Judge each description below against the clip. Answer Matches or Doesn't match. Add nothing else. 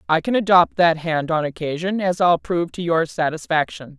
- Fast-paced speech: Doesn't match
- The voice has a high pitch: Doesn't match